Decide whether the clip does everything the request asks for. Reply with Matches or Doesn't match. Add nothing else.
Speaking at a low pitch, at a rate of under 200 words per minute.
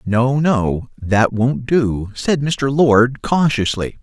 Matches